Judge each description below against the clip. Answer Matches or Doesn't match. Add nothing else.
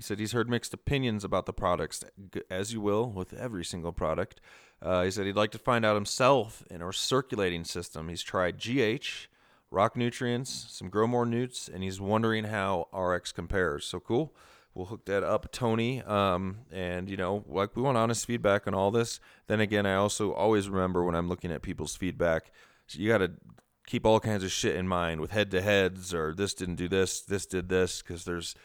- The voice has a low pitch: Matches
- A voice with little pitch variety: Doesn't match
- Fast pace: Matches